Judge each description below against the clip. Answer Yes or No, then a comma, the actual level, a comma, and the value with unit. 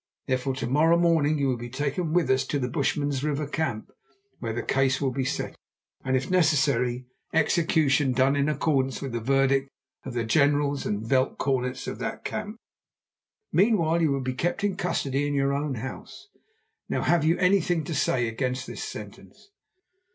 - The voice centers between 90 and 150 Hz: Yes, medium, 140 Hz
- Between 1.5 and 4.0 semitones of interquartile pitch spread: Yes, average, 3.3 semitones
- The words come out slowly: No, average, 180 wpm